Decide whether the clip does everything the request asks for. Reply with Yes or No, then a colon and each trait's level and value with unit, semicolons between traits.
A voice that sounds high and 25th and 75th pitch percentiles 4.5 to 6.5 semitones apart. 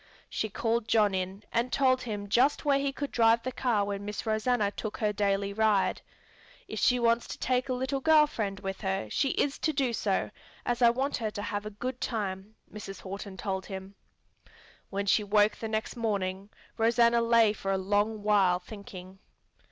No: high, 215 Hz; average, 3.1 semitones